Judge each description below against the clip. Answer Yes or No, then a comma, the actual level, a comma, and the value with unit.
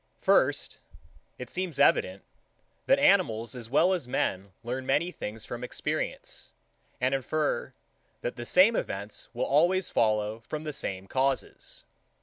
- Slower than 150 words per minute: Yes, average, 140 wpm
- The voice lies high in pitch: No, low, 125 Hz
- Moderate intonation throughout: No, wide, 5.7 semitones